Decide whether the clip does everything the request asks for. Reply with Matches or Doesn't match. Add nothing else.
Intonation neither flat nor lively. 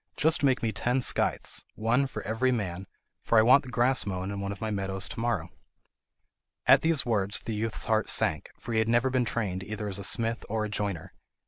Matches